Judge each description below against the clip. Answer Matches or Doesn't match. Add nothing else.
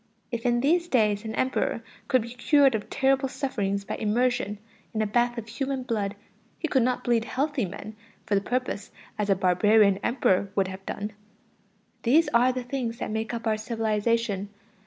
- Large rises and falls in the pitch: Doesn't match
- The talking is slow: Doesn't match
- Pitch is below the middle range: Doesn't match